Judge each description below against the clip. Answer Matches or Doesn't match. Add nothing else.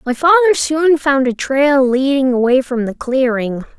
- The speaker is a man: Doesn't match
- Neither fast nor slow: Matches